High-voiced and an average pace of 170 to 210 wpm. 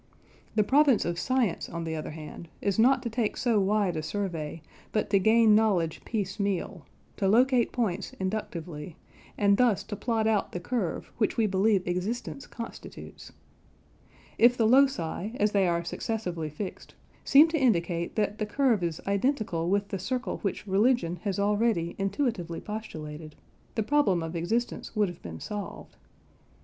No: high, 205 Hz; average, 160 wpm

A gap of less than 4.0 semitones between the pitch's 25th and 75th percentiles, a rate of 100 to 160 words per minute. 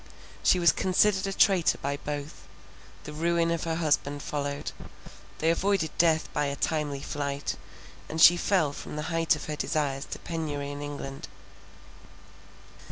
Yes: average, 2.7 semitones; average, 155 wpm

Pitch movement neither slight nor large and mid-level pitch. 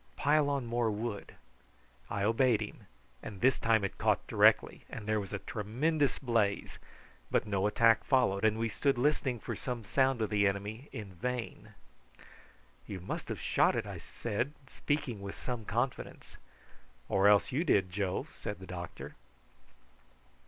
No: average, 3.8 semitones; low, 110 Hz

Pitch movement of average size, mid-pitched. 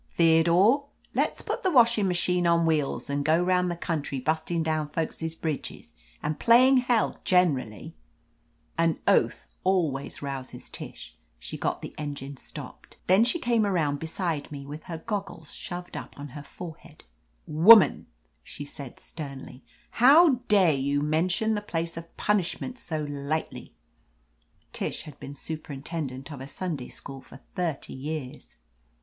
Yes: average, 4.2 semitones; medium, 160 Hz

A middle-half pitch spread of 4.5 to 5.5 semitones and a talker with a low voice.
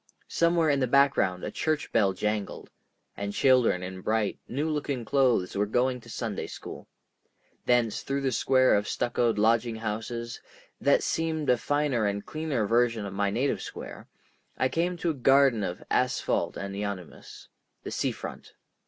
Yes: average, 5.0 semitones; low, 120 Hz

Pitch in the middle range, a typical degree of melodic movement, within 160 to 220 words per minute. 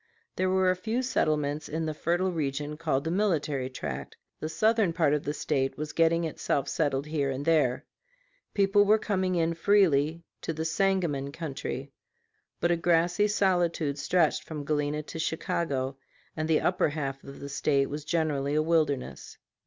Yes: medium, 155 Hz; average, 3.7 semitones; average, 170 wpm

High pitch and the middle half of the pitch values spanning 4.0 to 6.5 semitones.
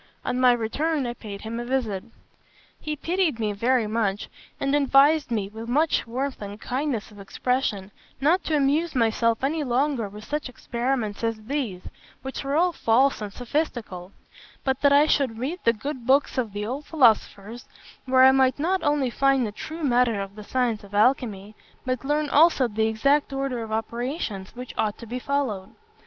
Yes: very high, 250 Hz; average, 4.3 semitones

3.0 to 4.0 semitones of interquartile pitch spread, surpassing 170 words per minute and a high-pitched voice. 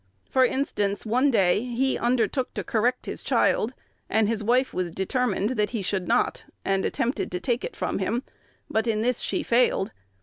Yes: average, 3.6 semitones; average, 180 wpm; high, 230 Hz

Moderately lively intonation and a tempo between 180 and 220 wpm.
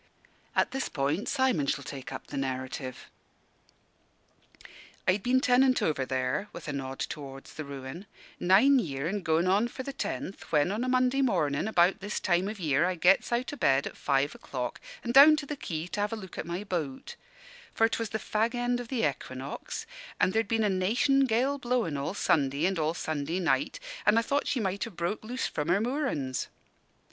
No: wide, 8.5 semitones; average, 200 wpm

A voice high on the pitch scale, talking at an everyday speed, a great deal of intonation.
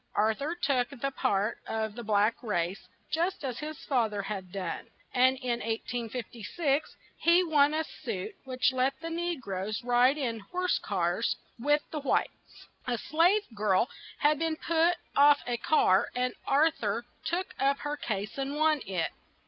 Yes: very high, 260 Hz; average, 165 wpm; wide, 5.8 semitones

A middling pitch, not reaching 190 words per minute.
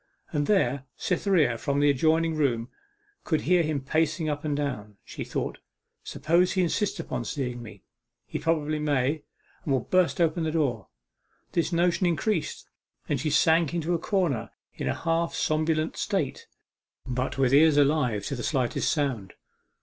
Yes: medium, 155 Hz; average, 160 wpm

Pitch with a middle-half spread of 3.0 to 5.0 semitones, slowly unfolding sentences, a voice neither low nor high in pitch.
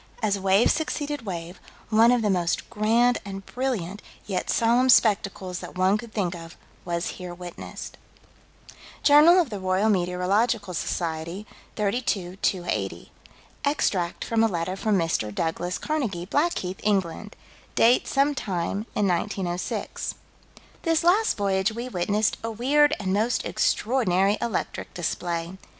No: average, 4.7 semitones; slow, 130 wpm; high, 200 Hz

